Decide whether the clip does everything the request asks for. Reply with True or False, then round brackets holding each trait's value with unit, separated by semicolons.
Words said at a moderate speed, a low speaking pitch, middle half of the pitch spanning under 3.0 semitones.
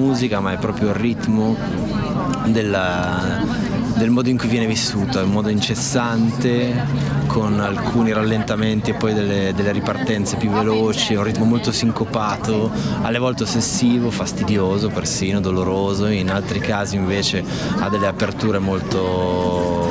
True (140 wpm; 105 Hz; 2.6 semitones)